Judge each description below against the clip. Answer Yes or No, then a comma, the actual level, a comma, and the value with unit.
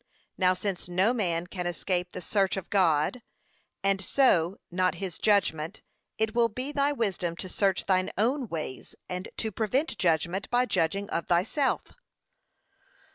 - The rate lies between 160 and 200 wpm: No, average, 150 wpm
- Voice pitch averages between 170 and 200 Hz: Yes, high, 190 Hz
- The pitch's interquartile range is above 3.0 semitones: Yes, average, 3.8 semitones